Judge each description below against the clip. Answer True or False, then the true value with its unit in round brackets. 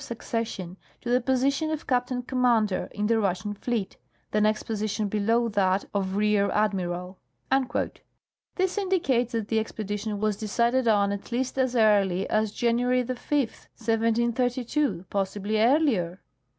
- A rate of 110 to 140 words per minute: True (135 wpm)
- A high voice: True (220 Hz)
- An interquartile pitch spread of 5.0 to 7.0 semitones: False (3.4 semitones)